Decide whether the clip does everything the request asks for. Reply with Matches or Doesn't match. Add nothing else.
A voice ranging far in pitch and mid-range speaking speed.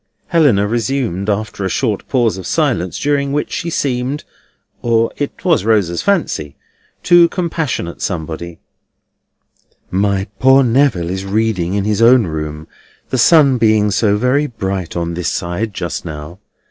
Matches